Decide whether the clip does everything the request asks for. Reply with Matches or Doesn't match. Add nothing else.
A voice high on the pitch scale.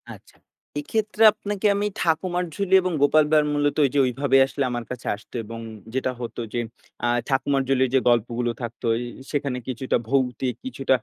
Doesn't match